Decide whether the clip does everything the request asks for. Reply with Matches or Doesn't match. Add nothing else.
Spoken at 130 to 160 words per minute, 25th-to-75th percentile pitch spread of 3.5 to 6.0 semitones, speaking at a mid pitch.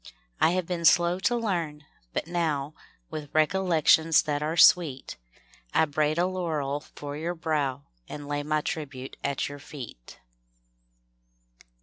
Doesn't match